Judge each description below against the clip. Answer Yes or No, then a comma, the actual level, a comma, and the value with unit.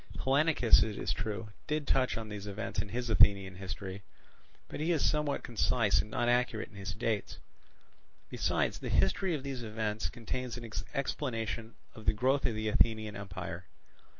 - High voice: No, low, 110 Hz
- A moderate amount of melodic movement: Yes, average, 3.5 semitones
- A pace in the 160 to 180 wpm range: Yes, average, 170 wpm